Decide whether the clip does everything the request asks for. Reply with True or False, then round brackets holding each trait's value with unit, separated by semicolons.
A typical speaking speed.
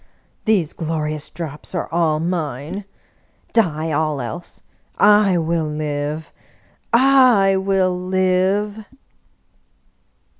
False (85 wpm)